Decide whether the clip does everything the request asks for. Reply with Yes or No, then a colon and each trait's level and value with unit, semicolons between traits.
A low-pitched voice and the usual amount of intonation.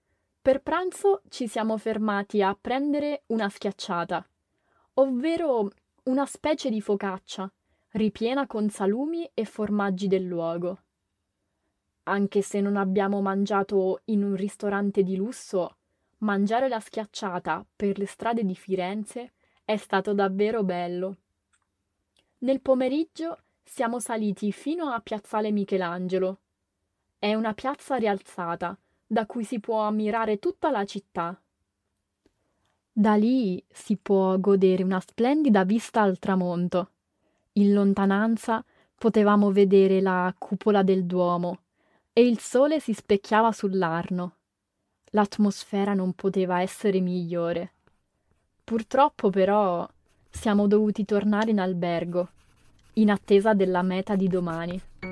No: high, 200 Hz; average, 3.1 semitones